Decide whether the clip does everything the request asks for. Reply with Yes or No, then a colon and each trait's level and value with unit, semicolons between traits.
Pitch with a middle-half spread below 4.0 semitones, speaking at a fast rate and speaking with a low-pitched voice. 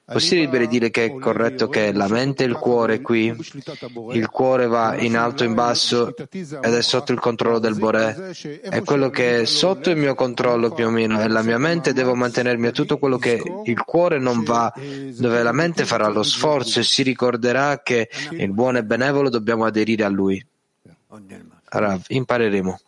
Yes: average, 2.9 semitones; fast, 195 wpm; low, 120 Hz